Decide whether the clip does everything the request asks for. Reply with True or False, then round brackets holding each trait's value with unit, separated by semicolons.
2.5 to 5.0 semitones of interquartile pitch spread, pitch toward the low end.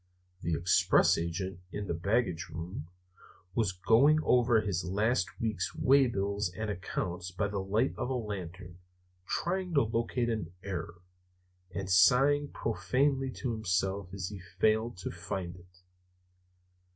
True (4.4 semitones; 100 Hz)